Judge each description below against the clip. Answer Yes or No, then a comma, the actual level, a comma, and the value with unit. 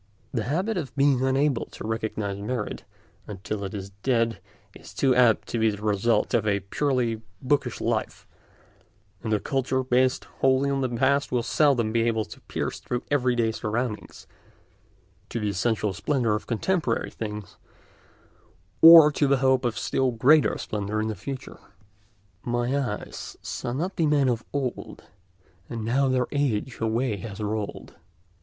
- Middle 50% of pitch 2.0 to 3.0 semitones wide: No, average, 3.7 semitones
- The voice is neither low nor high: No, low, 120 Hz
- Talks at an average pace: Yes, average, 155 wpm